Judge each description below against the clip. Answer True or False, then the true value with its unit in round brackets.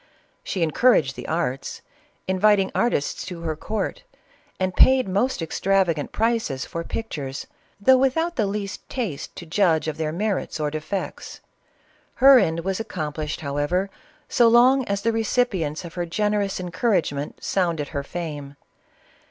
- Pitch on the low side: False (185 Hz)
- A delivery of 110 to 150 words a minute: True (140 wpm)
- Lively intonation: True (5.7 semitones)